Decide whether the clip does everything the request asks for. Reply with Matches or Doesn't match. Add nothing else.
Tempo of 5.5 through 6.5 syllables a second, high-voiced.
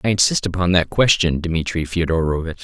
Doesn't match